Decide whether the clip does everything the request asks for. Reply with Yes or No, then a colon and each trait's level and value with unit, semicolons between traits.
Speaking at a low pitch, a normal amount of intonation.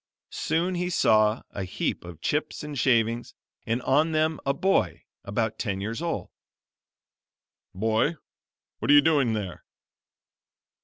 No: low, 120 Hz; wide, 6.3 semitones